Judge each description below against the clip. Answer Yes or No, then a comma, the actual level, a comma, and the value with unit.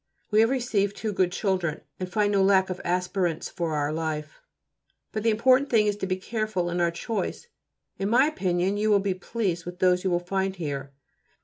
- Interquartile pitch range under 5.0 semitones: Yes, average, 3.4 semitones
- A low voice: No, high, 190 Hz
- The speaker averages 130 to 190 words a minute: No, fast, 205 wpm